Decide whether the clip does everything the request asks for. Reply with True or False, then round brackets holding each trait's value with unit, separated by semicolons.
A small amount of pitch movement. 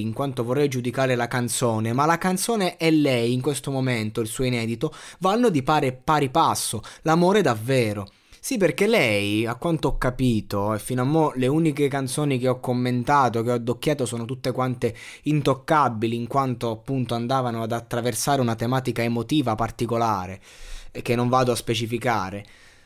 False (3.7 semitones)